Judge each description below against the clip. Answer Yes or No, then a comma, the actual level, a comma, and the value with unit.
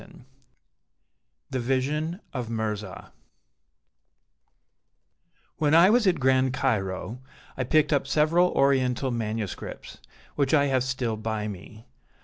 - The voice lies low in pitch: Yes, low, 130 Hz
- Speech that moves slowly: Yes, slow, 115 wpm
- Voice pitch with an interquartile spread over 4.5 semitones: Yes, average, 5.0 semitones